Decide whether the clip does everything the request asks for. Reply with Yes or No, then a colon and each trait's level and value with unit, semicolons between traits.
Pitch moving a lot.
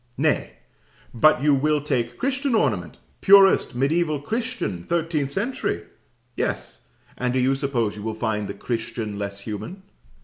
Yes: wide, 7.3 semitones